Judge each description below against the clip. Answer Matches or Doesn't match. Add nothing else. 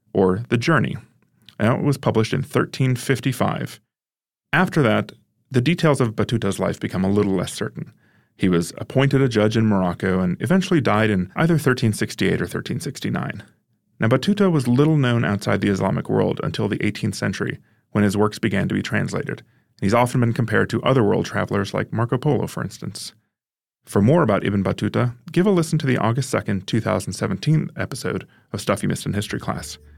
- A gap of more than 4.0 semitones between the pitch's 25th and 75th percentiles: Matches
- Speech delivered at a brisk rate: Doesn't match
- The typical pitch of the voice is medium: Doesn't match